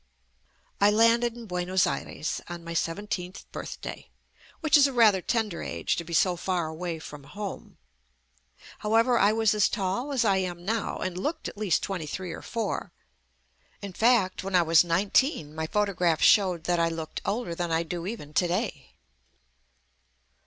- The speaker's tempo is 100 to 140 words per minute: No, average, 170 wpm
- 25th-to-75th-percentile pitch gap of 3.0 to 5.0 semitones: Yes, average, 4.4 semitones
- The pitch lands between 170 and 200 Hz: Yes, medium, 185 Hz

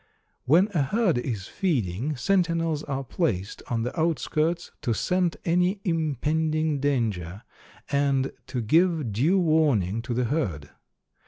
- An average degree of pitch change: No, wide, 5.7 semitones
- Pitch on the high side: No, medium, 145 Hz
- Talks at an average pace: No, slow, 130 wpm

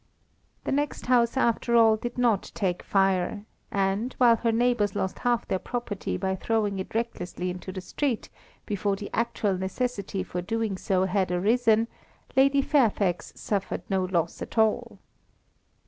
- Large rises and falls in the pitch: No, average, 3.8 semitones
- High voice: Yes, high, 210 Hz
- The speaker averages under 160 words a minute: Yes, average, 150 wpm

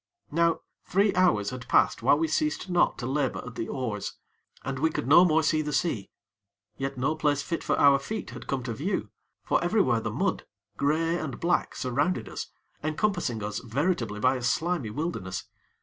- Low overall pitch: No, medium, 145 Hz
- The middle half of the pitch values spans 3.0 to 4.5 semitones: No, average, 5.2 semitones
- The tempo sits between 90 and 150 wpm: No, average, 185 wpm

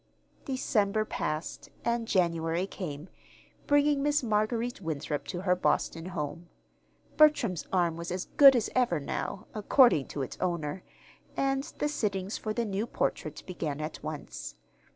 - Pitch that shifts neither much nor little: No, wide, 6.4 semitones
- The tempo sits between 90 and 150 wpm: Yes, average, 140 wpm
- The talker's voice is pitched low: No, high, 190 Hz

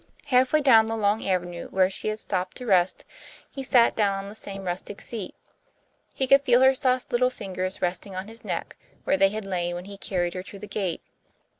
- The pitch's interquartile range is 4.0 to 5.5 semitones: Yes, average, 4.5 semitones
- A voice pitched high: Yes, high, 200 Hz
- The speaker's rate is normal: No, fast, 215 wpm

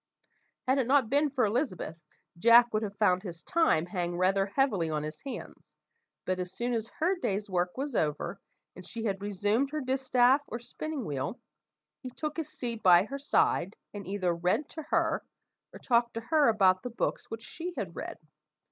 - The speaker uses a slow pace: No, average, 190 wpm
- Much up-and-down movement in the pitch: Yes, wide, 6.2 semitones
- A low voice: No, high, 220 Hz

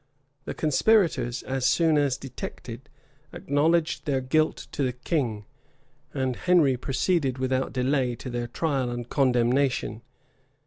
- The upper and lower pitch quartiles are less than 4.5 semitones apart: Yes, average, 2.9 semitones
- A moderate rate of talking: No, slow, 130 wpm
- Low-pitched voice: Yes, low, 130 Hz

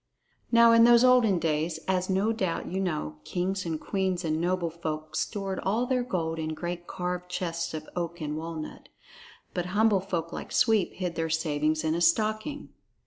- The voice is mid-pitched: Yes, medium, 180 Hz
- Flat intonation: No, average, 3.4 semitones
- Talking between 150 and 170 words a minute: No, average, 180 wpm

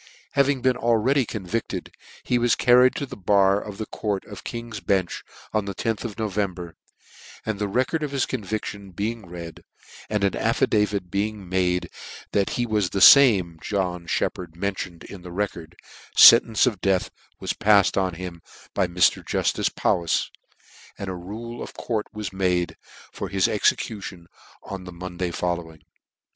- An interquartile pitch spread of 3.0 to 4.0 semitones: Yes, average, 3.5 semitones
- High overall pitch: No, low, 100 Hz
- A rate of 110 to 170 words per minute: Yes, average, 160 wpm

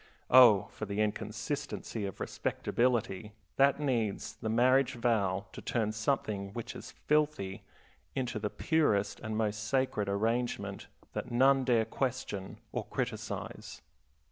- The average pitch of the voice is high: No, low, 115 Hz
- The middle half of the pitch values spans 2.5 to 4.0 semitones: Yes, average, 3.7 semitones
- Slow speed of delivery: Yes, slow, 125 wpm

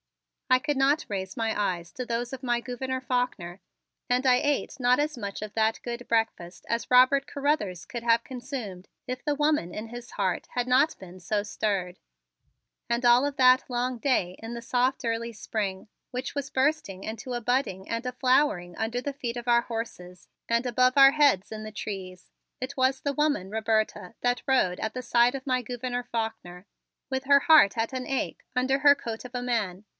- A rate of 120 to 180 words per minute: No, average, 195 wpm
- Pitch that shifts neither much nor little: Yes, average, 3.2 semitones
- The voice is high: Yes, high, 240 Hz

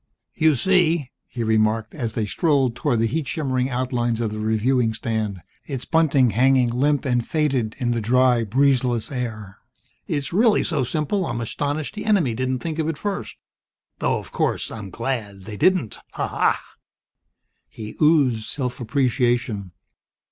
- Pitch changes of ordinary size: Yes, average, 4.5 semitones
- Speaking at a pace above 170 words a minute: No, average, 155 wpm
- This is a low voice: Yes, low, 125 Hz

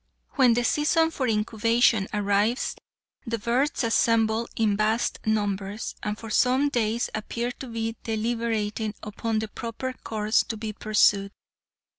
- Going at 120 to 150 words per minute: Yes, slow, 135 wpm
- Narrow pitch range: Yes, narrow, 1.9 semitones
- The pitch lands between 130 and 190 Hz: No, high, 225 Hz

